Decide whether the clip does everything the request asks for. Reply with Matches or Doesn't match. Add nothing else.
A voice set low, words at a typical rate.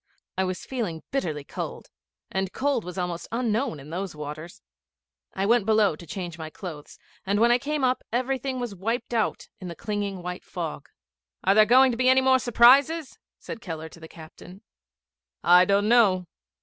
Doesn't match